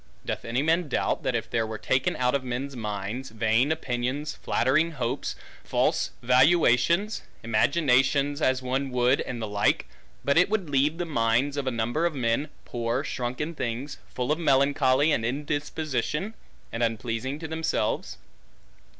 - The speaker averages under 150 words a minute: No, average, 155 wpm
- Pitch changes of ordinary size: Yes, average, 3.9 semitones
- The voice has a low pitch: Yes, low, 130 Hz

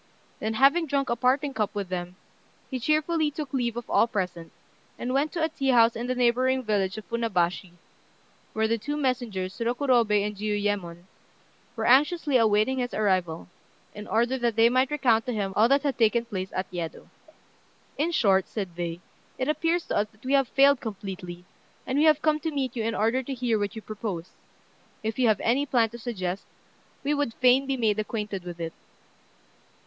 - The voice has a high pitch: Yes, high, 230 Hz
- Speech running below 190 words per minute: No, average, 195 wpm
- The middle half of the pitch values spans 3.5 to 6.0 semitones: Yes, average, 4.4 semitones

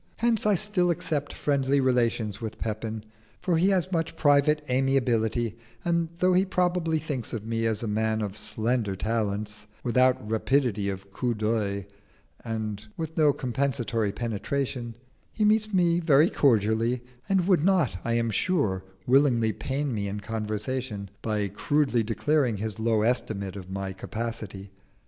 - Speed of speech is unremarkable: Yes, average, 150 wpm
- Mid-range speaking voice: No, low, 120 Hz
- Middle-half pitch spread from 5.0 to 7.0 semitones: Yes, wide, 5.4 semitones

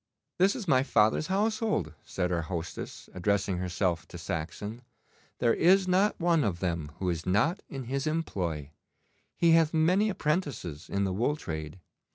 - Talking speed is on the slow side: No, average, 160 wpm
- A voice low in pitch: Yes, low, 110 Hz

